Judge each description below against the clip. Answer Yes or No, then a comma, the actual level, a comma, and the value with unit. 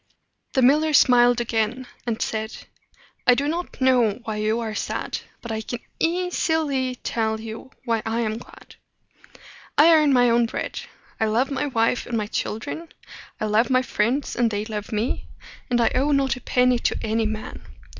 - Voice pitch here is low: No, high, 240 Hz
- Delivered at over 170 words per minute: Yes, average, 180 wpm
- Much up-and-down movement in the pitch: No, average, 3.3 semitones